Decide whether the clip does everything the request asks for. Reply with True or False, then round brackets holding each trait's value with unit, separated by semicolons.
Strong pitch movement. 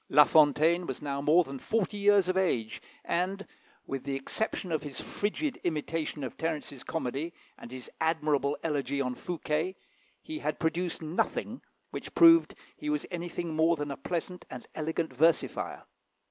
False (4.0 semitones)